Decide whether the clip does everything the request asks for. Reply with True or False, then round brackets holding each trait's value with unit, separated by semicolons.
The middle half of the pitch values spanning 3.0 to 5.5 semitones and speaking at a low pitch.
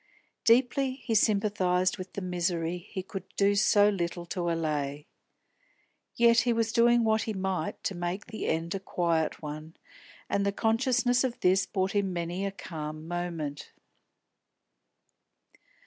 False (4.2 semitones; 190 Hz)